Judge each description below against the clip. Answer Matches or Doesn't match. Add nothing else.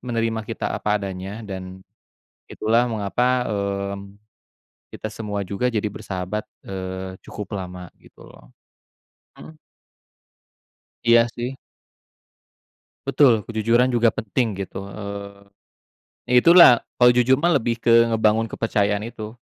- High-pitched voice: Doesn't match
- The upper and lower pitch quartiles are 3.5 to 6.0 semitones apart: Doesn't match